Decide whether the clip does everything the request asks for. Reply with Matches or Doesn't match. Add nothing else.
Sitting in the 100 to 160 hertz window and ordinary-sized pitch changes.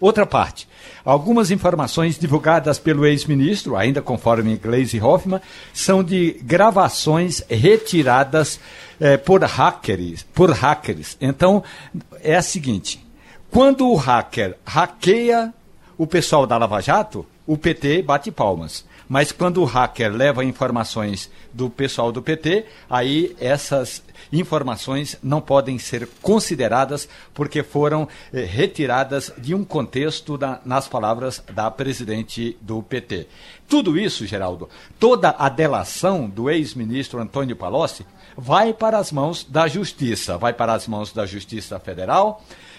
Doesn't match